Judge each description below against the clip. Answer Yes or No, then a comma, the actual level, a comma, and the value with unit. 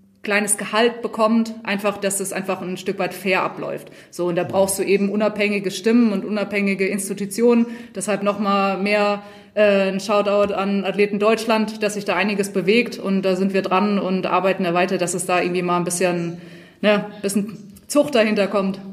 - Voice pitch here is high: Yes, high, 200 Hz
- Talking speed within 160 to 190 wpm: Yes, average, 185 wpm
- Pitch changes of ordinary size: No, narrow, 1.5 semitones